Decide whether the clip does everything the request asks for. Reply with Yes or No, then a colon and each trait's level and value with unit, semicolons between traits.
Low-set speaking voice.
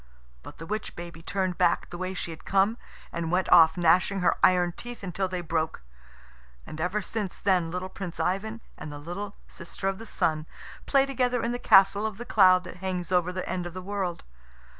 No: medium, 185 Hz